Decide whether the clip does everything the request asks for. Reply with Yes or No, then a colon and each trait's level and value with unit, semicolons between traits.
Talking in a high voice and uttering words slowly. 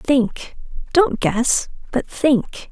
Yes: very high, 275 Hz; slow, 110 wpm